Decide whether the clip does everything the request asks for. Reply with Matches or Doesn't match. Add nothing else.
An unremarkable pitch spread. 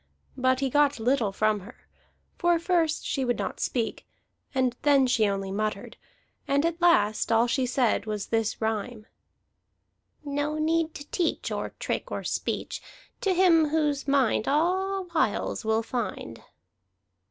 Doesn't match